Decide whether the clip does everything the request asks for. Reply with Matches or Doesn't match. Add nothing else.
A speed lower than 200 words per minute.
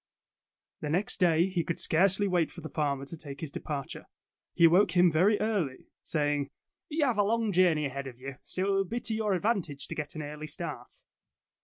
Doesn't match